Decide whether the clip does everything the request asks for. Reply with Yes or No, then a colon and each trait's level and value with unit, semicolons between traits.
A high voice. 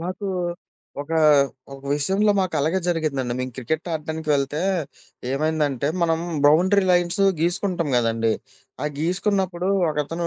No: medium, 160 Hz